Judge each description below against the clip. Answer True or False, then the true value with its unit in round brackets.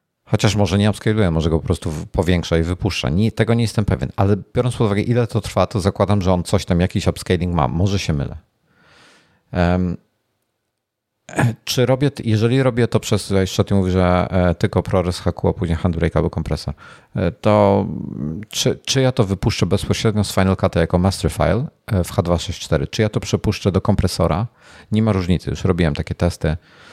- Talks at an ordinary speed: False (185 wpm)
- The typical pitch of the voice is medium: False (100 Hz)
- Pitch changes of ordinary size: True (3.5 semitones)